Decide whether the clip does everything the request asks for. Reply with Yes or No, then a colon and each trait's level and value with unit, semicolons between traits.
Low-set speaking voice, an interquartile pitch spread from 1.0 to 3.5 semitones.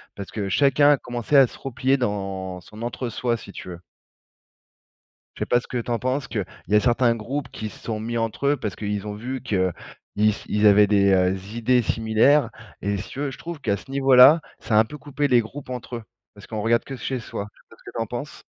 No: low, 115 Hz; average, 3.9 semitones